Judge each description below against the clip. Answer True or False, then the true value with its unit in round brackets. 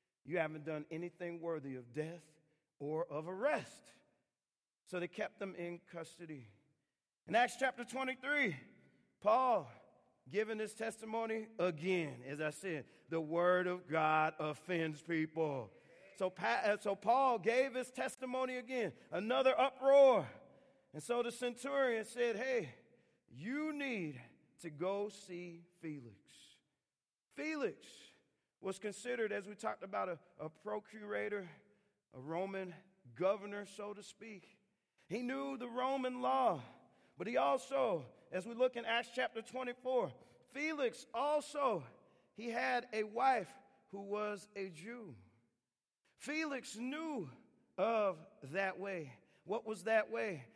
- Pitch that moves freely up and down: True (6.5 semitones)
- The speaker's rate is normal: False (125 wpm)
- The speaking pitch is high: True (205 Hz)